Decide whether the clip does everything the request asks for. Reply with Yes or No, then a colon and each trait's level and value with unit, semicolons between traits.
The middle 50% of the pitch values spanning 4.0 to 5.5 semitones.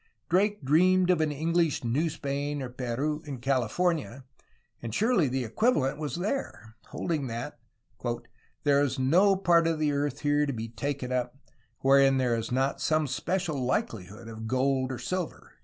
Yes: average, 4.3 semitones